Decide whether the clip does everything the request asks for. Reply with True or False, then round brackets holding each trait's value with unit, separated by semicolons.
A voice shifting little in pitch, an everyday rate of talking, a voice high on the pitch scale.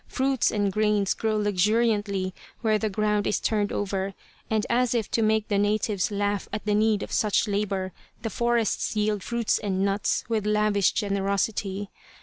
True (1.5 semitones; 165 wpm; 210 Hz)